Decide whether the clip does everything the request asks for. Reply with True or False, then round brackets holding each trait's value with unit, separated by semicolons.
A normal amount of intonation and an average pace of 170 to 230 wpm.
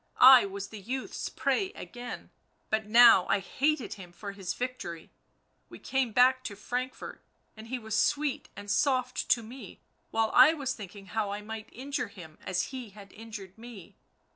True (4.2 semitones; 175 wpm)